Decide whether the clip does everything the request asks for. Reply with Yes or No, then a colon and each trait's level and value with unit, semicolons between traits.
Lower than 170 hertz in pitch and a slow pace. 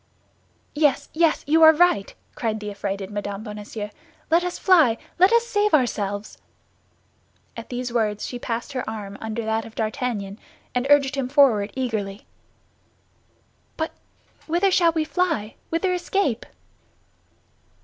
No: high, 245 Hz; slow, 130 wpm